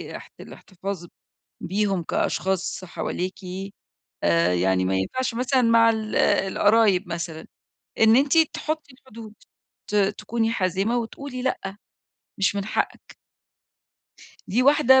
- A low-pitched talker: No, high, 210 Hz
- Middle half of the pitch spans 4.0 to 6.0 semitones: Yes, average, 4.4 semitones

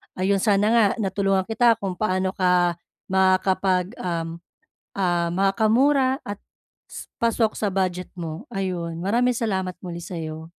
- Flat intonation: No, average, 3.1 semitones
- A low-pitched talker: No, high, 190 Hz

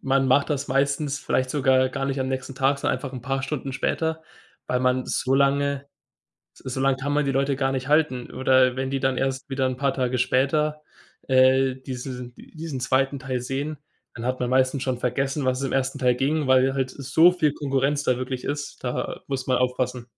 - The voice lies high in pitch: No, low, 135 Hz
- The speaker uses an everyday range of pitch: No, narrow, 1.4 semitones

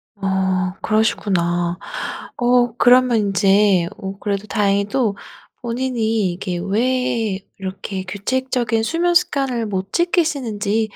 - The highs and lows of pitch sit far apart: No, average, 4.3 semitones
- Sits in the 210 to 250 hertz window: Yes, high, 215 Hz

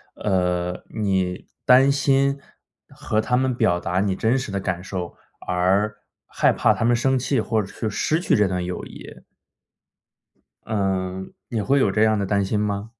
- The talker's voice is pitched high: No, low, 105 Hz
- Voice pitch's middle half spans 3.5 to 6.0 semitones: Yes, average, 4.4 semitones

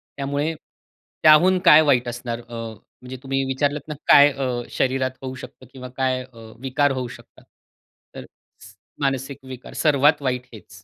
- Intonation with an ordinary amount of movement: No, narrow, 2.1 semitones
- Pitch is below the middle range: Yes, low, 130 Hz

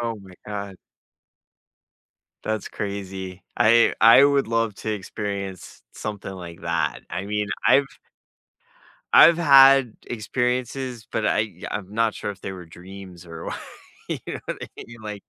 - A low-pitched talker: Yes, low, 105 Hz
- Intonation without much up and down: No, average, 3.4 semitones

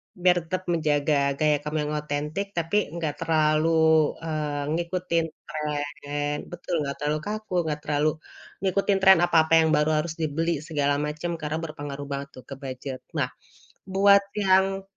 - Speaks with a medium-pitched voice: Yes, medium, 155 Hz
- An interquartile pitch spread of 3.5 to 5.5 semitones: No, average, 2.8 semitones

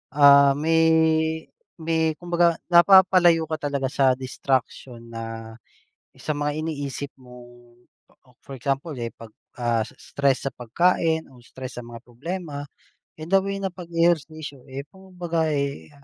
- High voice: No, medium, 145 Hz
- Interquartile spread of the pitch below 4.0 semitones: No, average, 4.3 semitones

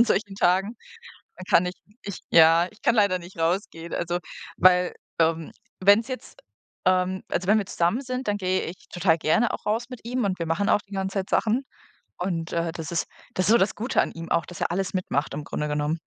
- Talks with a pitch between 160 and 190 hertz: Yes, medium, 185 Hz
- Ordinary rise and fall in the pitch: Yes, average, 3.6 semitones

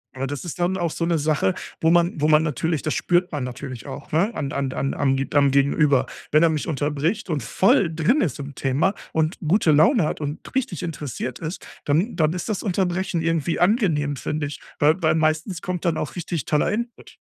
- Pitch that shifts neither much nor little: Yes, average, 3.4 semitones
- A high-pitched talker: No, medium, 155 Hz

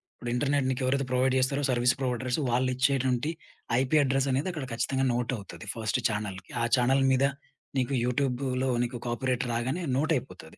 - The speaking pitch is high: No, low, 130 Hz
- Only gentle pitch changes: Yes, narrow, 1.8 semitones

